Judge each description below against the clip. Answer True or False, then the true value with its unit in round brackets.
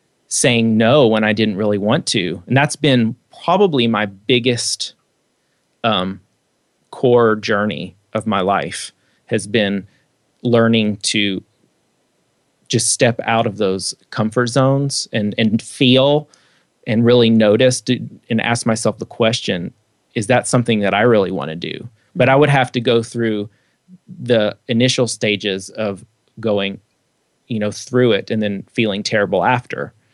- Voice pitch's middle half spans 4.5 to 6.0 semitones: False (3.0 semitones)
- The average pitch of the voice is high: False (115 Hz)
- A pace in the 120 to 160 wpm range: True (145 wpm)